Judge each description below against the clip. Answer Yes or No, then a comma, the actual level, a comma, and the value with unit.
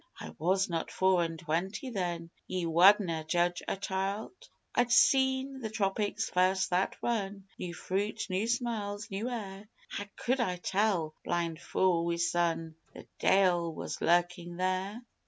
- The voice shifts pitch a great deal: No, average, 3.2 semitones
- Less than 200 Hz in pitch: Yes, high, 190 Hz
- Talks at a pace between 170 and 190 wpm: No, average, 150 wpm